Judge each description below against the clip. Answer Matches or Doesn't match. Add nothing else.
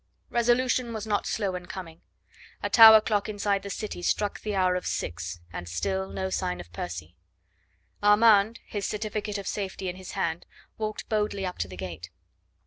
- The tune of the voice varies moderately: Matches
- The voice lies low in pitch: Doesn't match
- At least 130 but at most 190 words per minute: Matches